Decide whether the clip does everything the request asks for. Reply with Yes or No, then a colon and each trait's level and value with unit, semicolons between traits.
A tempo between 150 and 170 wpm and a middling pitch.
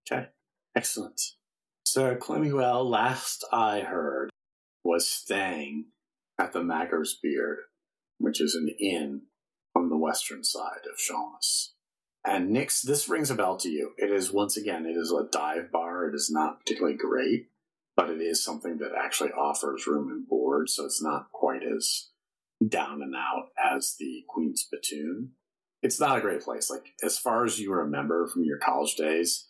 No: average, 165 wpm; low, 105 Hz